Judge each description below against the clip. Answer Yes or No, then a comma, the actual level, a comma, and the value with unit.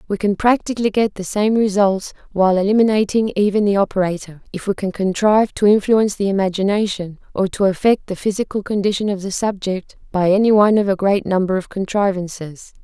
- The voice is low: No, high, 200 Hz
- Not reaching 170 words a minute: No, average, 180 wpm